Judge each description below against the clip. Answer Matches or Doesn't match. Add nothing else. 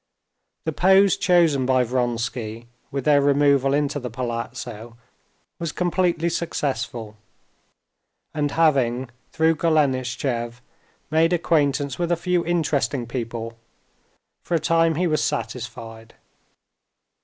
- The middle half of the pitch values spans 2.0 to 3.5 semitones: Doesn't match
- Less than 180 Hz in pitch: Matches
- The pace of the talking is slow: Matches